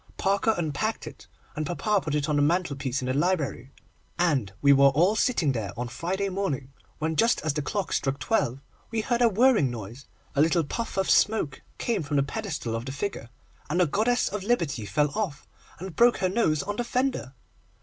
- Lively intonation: Yes, wide, 6.8 semitones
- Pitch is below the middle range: No, medium, 160 Hz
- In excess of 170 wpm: Yes, average, 200 wpm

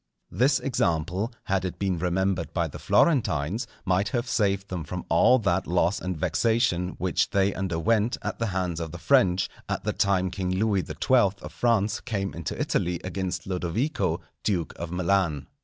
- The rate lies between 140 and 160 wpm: No, average, 170 wpm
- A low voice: Yes, very low, 95 Hz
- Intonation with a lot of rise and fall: No, average, 3.2 semitones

